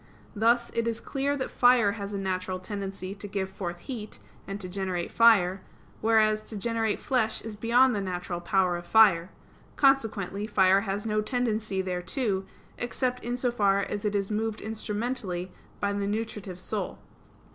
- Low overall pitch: No, high, 205 Hz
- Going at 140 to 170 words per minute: Yes, average, 165 wpm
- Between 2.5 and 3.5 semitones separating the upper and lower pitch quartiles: Yes, average, 3.1 semitones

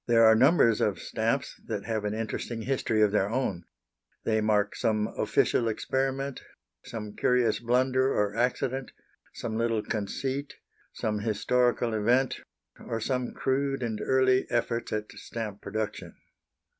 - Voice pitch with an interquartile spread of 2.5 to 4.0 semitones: Yes, average, 3.2 semitones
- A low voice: Yes, low, 115 Hz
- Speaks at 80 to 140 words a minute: Yes, slow, 135 wpm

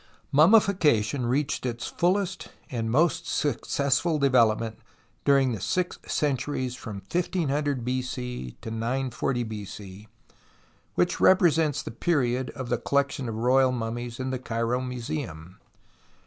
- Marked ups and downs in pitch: No, average, 3.9 semitones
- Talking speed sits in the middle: No, slow, 125 wpm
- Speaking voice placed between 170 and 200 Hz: No, low, 130 Hz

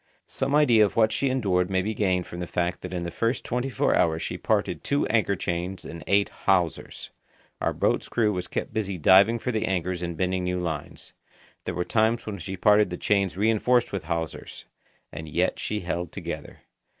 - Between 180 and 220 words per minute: Yes, average, 200 wpm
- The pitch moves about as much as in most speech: Yes, average, 3.7 semitones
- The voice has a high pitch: No, very low, 95 Hz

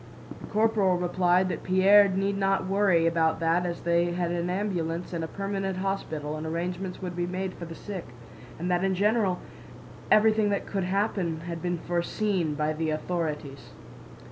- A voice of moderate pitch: Yes, medium, 180 Hz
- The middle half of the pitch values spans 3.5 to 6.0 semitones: No, narrow, 2.6 semitones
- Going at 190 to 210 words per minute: No, average, 170 wpm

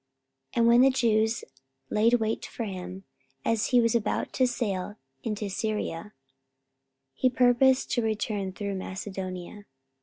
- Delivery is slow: Yes, slow, 130 wpm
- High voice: Yes, high, 215 Hz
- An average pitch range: Yes, average, 3.3 semitones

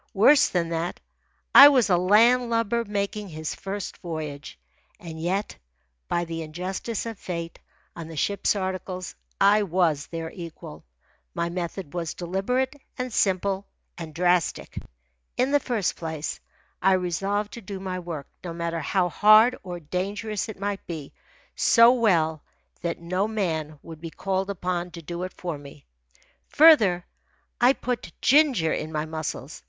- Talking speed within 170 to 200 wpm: No, average, 150 wpm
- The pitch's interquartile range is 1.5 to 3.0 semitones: No, average, 3.8 semitones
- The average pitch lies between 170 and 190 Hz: Yes, medium, 185 Hz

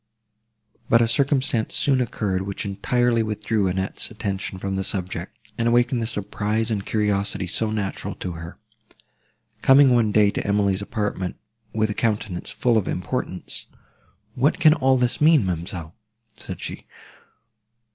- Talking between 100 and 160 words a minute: Yes, average, 145 wpm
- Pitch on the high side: No, low, 105 Hz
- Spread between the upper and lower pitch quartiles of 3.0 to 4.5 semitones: Yes, average, 3.7 semitones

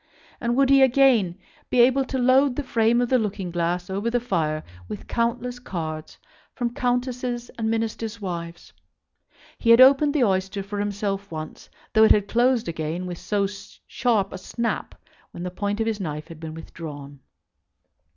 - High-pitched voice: Yes, high, 215 Hz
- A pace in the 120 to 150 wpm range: No, average, 170 wpm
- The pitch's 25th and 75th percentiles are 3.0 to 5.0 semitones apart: No, wide, 5.5 semitones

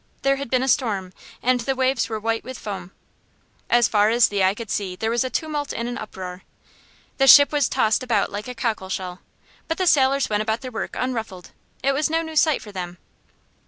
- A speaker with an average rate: No, fast, 220 wpm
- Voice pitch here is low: No, high, 235 Hz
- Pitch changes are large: No, average, 4.6 semitones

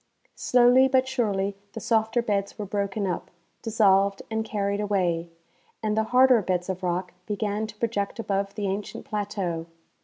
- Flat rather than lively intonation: Yes, narrow, 2.3 semitones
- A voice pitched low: No, high, 205 Hz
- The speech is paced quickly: No, average, 160 wpm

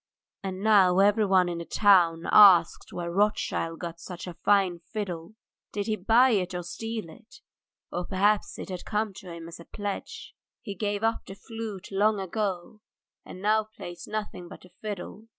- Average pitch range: Yes, average, 3.2 semitones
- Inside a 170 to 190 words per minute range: Yes, average, 175 wpm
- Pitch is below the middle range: No, high, 195 Hz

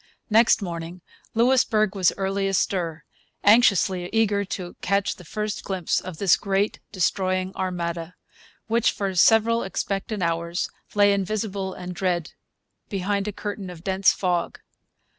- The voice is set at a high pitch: Yes, high, 195 Hz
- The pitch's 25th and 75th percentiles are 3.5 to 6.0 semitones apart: No, narrow, 2.4 semitones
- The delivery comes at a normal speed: No, slow, 130 wpm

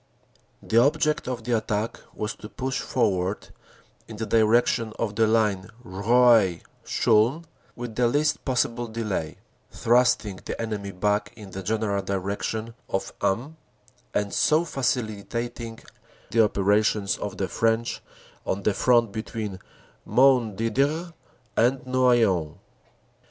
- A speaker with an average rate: No, slow, 125 wpm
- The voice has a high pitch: No, low, 110 Hz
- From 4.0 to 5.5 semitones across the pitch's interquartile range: No, average, 3.1 semitones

